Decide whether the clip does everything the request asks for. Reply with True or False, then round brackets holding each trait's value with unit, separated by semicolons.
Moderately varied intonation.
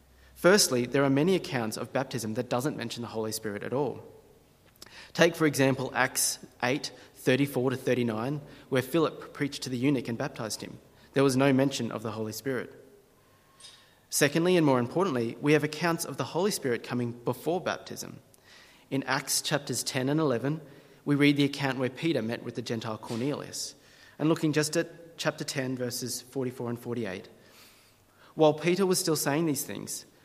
True (3.5 semitones)